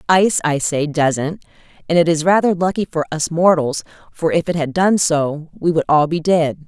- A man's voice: No, female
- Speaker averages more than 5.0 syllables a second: No, 4.9 syllables/s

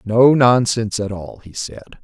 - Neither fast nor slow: Yes, average, 175 wpm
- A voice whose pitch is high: No, low, 110 Hz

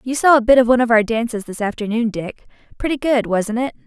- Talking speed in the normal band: No, fast, 235 wpm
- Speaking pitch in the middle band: No, high, 235 Hz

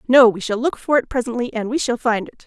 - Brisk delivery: Yes, fast, 290 wpm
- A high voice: Yes, high, 240 Hz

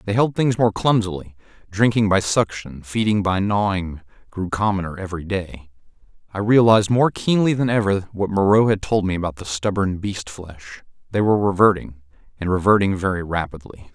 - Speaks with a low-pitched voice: Yes, low, 100 Hz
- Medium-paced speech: Yes, average, 165 wpm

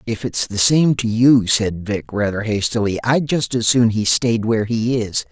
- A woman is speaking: No, male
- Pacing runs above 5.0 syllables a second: No, 4.5 syllables/s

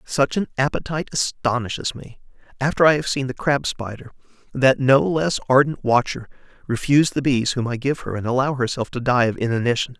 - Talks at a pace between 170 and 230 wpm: Yes, average, 185 wpm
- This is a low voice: Yes, low, 130 Hz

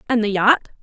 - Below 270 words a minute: Yes, fast, 215 wpm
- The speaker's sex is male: No, female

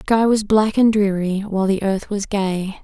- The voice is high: Yes, high, 200 Hz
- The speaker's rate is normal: No, fast, 235 wpm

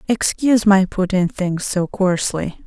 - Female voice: Yes, female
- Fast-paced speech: No, slow, 135 wpm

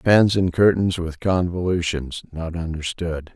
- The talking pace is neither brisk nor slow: No, slow, 105 wpm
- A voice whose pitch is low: Yes, very low, 85 Hz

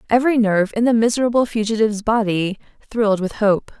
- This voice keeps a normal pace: Yes, average, 160 wpm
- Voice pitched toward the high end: Yes, high, 220 Hz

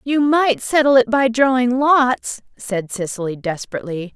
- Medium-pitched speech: No, high, 245 Hz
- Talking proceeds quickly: No, average, 145 wpm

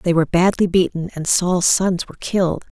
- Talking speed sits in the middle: Yes, average, 195 wpm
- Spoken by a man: No, female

